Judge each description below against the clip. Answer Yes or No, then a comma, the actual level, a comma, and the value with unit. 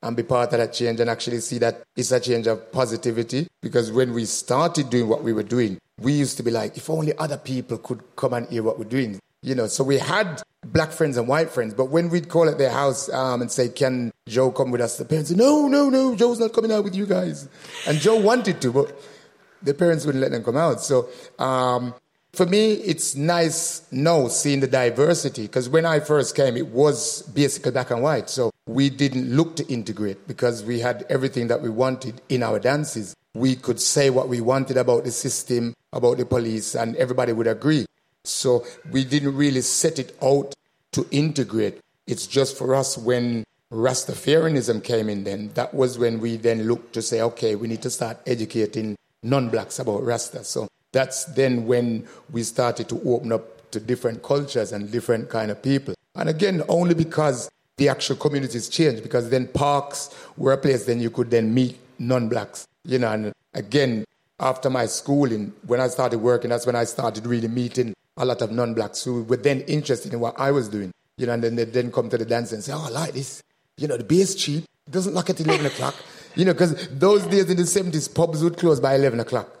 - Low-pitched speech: Yes, low, 130 Hz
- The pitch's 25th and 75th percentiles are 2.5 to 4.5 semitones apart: Yes, average, 4.0 semitones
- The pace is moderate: No, fast, 215 wpm